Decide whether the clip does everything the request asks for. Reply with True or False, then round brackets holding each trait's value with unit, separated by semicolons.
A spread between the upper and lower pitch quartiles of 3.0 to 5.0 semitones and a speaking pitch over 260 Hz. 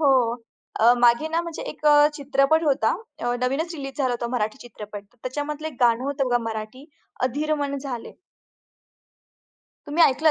True (3.5 semitones; 270 Hz)